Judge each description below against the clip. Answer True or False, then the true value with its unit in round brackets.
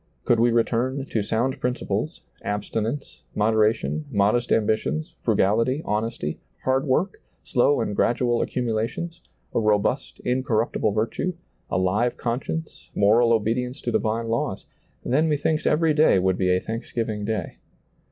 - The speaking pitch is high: False (115 Hz)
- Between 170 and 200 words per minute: False (135 wpm)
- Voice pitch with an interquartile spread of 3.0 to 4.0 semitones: True (3.4 semitones)